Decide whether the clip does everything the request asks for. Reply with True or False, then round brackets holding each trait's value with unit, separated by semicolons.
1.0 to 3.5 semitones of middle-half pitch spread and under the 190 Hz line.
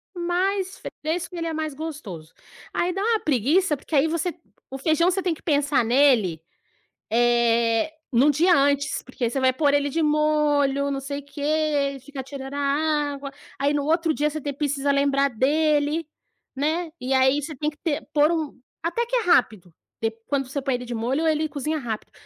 False (2.7 semitones; 285 Hz)